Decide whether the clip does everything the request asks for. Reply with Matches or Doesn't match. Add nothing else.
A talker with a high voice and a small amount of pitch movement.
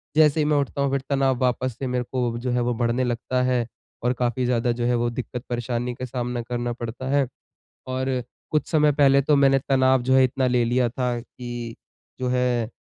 Doesn't match